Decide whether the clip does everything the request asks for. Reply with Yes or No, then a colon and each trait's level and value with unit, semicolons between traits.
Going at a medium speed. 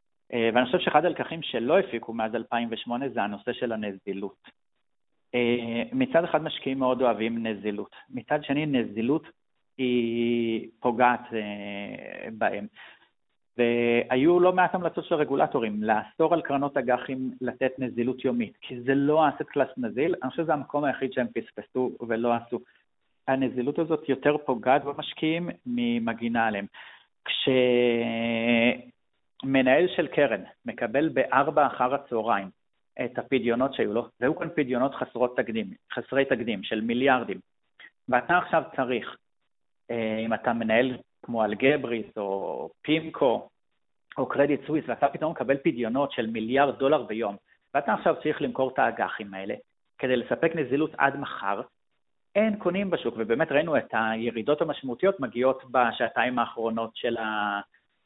Yes: average, 130 wpm